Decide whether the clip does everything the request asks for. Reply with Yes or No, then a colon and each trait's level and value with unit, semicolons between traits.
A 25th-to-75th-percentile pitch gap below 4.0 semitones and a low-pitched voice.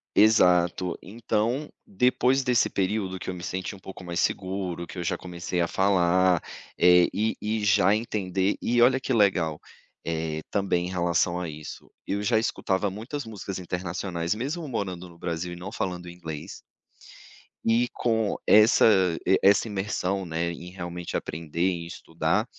Yes: average, 3.5 semitones; very low, 95 Hz